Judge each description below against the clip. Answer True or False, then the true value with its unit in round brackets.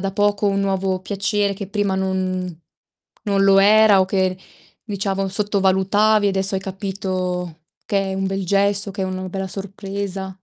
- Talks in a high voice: True (195 Hz)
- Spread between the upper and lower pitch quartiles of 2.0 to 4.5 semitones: False (1.0 semitones)